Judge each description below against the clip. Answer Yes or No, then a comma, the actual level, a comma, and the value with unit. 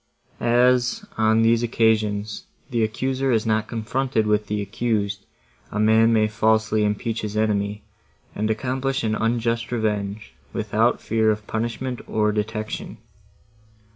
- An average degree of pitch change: No, narrow, 1.7 semitones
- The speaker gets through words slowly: Yes, slow, 130 wpm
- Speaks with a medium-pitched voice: No, low, 110 Hz